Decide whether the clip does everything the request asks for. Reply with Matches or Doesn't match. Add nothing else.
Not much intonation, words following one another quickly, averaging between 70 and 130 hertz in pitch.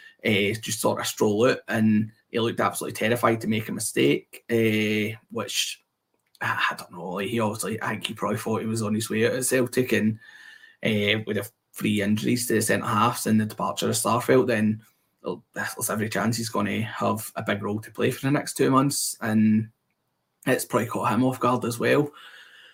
Matches